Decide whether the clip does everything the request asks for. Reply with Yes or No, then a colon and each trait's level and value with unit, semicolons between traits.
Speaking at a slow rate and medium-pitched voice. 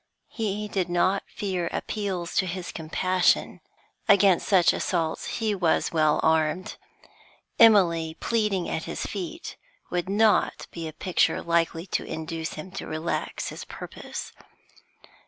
Yes: slow, 130 wpm; medium, 180 Hz